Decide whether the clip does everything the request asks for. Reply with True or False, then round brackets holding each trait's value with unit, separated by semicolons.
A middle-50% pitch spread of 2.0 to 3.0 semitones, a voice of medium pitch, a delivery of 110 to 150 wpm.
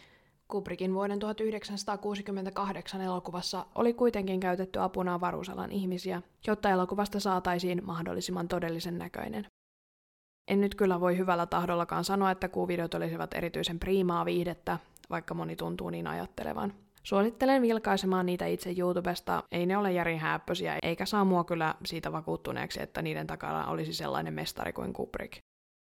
True (2.6 semitones; 180 Hz; 130 wpm)